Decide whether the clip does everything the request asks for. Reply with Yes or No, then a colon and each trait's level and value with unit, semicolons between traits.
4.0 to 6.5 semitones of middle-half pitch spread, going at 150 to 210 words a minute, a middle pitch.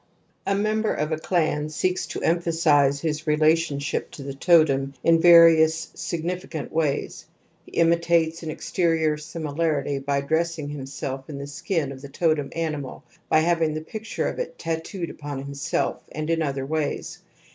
No: average, 2.7 semitones; average, 155 wpm; medium, 155 Hz